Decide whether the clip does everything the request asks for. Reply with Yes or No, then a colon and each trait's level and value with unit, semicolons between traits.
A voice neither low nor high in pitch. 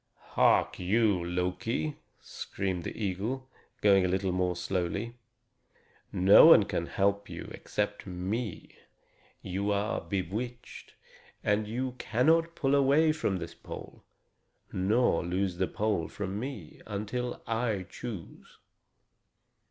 No: low, 100 Hz